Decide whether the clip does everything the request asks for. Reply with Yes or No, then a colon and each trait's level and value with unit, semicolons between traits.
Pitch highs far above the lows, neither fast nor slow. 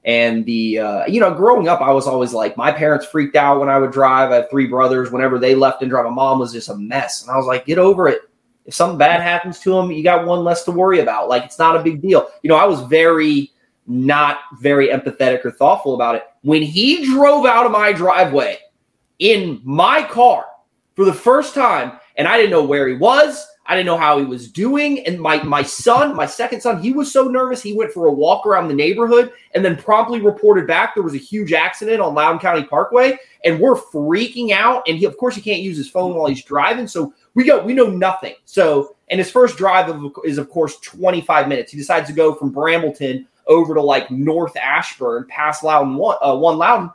No: wide, 8.2 semitones; fast, 235 wpm